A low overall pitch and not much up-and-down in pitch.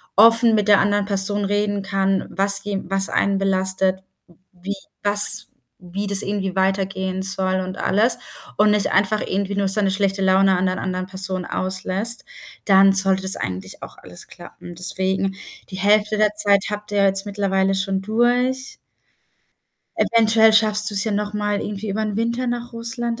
No: high, 200 Hz; narrow, 1.7 semitones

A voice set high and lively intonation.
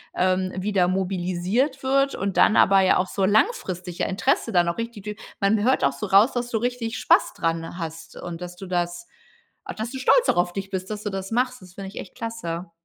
No: high, 195 Hz; average, 4.2 semitones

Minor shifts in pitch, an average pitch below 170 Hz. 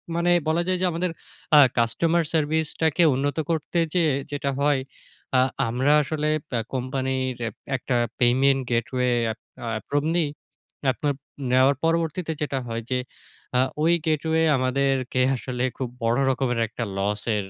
No: average, 4.0 semitones; medium, 140 Hz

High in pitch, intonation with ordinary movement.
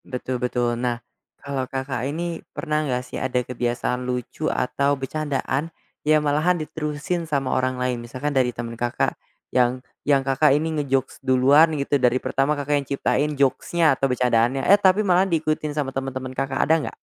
No: low, 135 Hz; average, 3.1 semitones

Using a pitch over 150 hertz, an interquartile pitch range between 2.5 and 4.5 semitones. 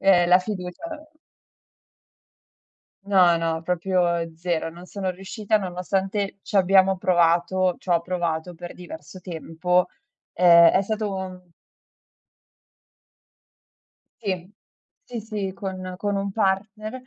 No: medium, 185 Hz; narrow, 2.0 semitones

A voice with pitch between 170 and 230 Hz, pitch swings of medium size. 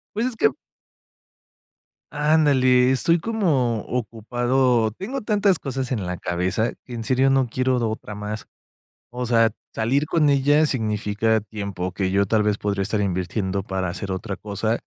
No: low, 115 Hz; average, 4.6 semitones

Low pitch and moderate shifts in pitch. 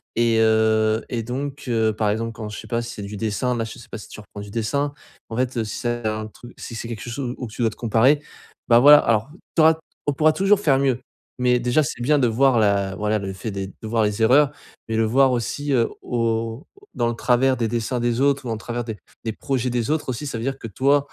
Yes: low, 120 Hz; average, 3.1 semitones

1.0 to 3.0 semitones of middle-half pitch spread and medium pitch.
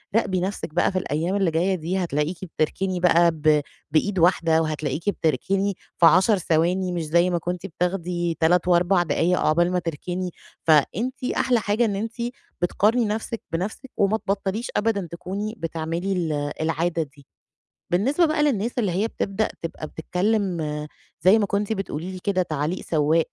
No: average, 3.4 semitones; medium, 180 Hz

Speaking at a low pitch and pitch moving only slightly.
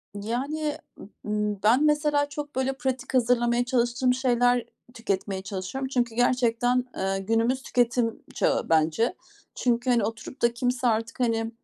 No: high, 240 Hz; narrow, 2.3 semitones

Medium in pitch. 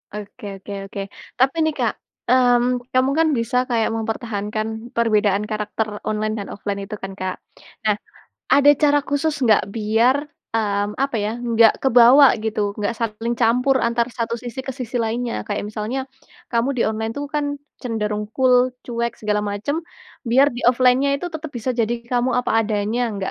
No: high, 230 Hz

